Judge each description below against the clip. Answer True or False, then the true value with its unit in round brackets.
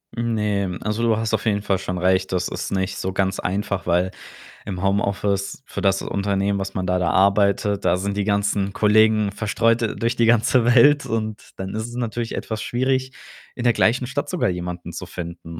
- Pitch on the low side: True (100 Hz)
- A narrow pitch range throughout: False (3.1 semitones)